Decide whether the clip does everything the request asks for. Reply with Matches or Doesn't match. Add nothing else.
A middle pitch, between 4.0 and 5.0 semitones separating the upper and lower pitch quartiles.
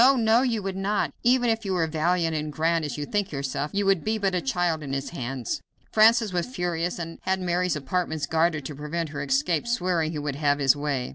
Matches